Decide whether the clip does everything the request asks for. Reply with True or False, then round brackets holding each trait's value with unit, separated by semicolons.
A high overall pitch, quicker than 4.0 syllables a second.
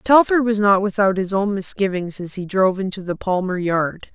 True (195 Hz; 5.1 syllables/s)